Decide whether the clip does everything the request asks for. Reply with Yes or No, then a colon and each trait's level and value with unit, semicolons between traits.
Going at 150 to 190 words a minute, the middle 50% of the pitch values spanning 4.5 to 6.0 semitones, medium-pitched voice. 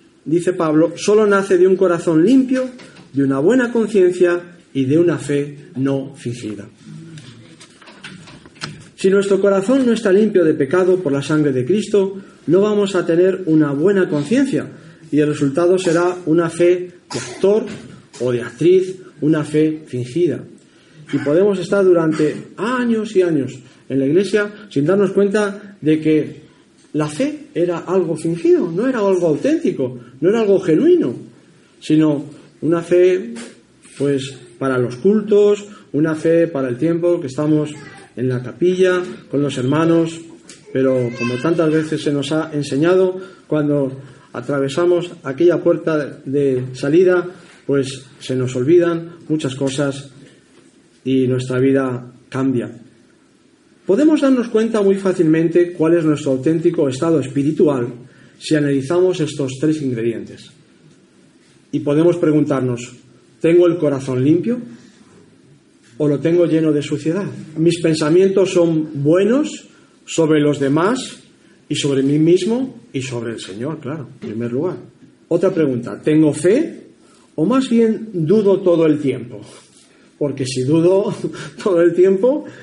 No: average, 135 wpm; average, 4.8 semitones; medium, 160 Hz